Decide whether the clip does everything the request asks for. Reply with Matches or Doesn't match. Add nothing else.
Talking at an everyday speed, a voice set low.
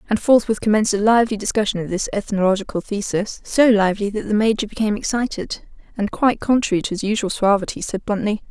Doesn't match